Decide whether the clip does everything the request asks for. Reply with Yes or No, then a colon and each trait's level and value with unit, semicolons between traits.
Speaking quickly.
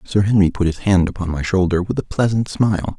Yes: fast, 240 wpm